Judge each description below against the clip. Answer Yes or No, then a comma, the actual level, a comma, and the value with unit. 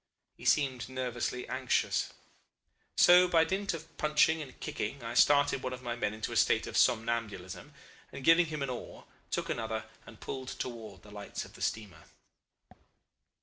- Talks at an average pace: Yes, average, 165 wpm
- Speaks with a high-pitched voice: No, low, 125 Hz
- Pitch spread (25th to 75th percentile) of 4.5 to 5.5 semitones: Yes, average, 5.2 semitones